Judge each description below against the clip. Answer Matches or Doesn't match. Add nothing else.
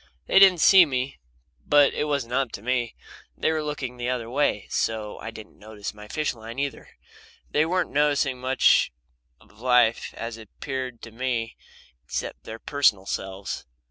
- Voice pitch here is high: Doesn't match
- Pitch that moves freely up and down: Doesn't match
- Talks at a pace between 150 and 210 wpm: Matches